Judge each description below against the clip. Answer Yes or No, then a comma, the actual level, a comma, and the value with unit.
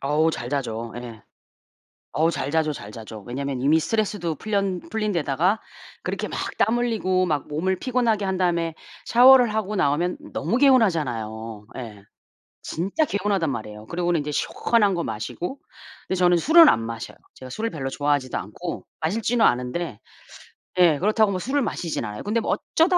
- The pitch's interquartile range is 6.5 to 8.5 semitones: Yes, wide, 8.0 semitones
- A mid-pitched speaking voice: Yes, medium, 170 Hz